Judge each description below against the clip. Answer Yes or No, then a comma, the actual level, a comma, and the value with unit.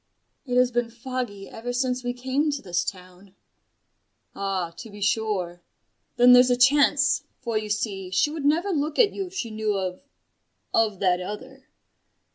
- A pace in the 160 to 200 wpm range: Yes, average, 170 wpm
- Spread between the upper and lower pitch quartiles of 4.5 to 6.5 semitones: Yes, average, 4.8 semitones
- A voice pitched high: Yes, high, 235 Hz